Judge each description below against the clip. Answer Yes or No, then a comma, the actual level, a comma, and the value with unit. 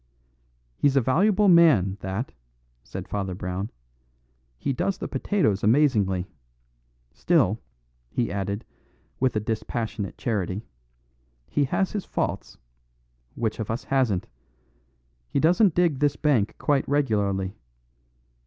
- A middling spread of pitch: No, wide, 6.7 semitones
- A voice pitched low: Yes, low, 115 Hz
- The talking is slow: Yes, slow, 115 wpm